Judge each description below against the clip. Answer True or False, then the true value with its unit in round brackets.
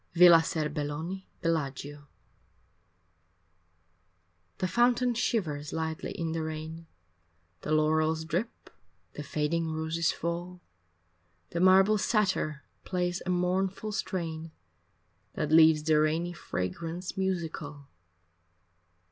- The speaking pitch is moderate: True (165 Hz)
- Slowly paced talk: True (95 wpm)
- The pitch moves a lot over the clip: False (2.8 semitones)